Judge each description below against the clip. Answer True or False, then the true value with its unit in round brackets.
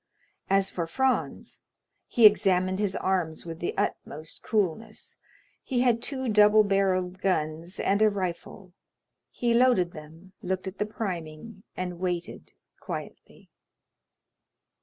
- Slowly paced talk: True (120 wpm)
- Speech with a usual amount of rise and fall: True (3.5 semitones)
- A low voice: False (190 Hz)